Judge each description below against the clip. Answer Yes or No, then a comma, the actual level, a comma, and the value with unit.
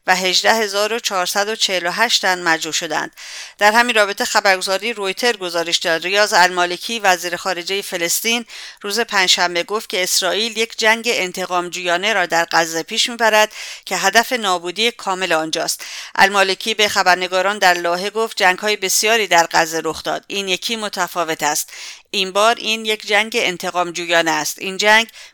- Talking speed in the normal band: Yes, average, 150 wpm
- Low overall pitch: No, high, 190 Hz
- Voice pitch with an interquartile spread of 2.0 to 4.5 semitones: Yes, average, 3.5 semitones